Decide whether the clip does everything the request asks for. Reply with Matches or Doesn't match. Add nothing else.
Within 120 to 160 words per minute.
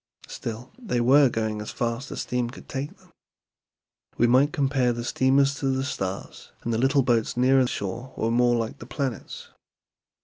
Doesn't match